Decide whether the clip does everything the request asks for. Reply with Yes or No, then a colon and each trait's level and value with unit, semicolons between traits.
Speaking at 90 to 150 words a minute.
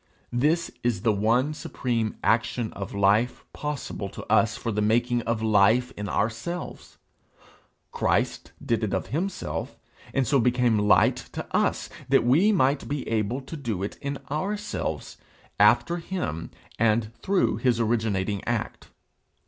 Yes: average, 140 wpm